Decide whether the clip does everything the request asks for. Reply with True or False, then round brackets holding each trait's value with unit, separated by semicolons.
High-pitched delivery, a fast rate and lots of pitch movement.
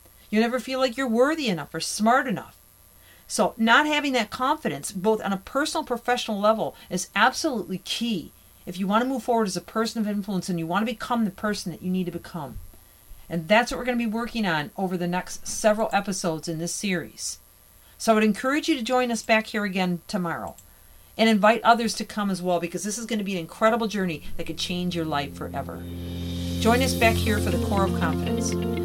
True (195 Hz; 225 wpm; 6.7 semitones)